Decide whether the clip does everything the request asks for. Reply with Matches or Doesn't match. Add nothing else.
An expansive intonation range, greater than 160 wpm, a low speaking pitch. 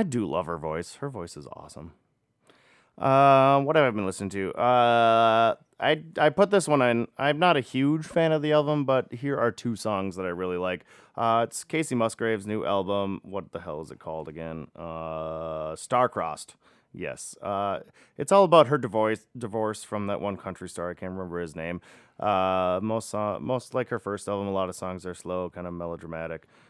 Matches